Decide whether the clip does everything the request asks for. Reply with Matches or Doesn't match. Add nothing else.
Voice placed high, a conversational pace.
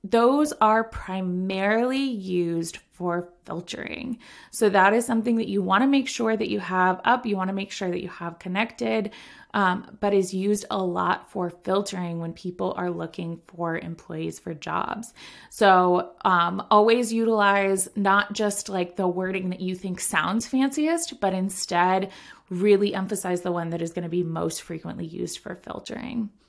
Matches